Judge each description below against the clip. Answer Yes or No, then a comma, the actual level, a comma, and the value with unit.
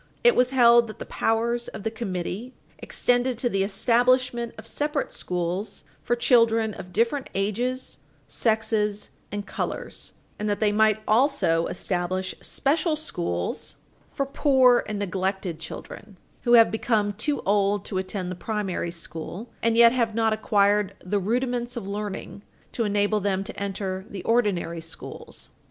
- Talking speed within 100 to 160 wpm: Yes, average, 150 wpm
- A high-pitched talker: Yes, high, 215 Hz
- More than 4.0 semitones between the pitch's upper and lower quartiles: No, average, 3.5 semitones